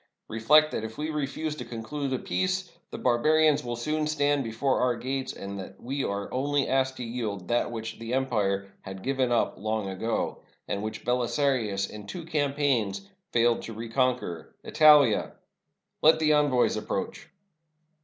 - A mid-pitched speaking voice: No, low, 125 Hz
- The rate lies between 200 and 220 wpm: No, average, 165 wpm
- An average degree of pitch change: Yes, average, 4.6 semitones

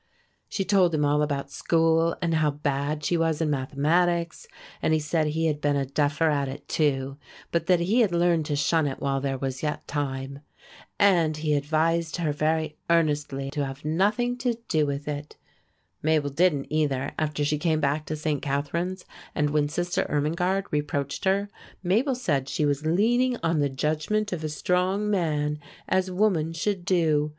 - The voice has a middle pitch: Yes, medium, 155 Hz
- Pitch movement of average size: Yes, average, 3.1 semitones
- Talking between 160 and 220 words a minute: Yes, average, 180 wpm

